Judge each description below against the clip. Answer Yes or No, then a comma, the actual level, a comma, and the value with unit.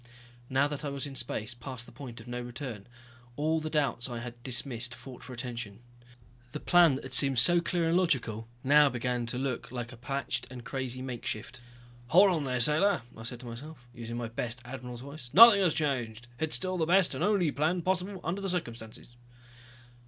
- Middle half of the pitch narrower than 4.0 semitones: No, average, 4.5 semitones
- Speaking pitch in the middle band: No, low, 130 Hz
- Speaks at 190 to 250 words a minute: Yes, fast, 205 wpm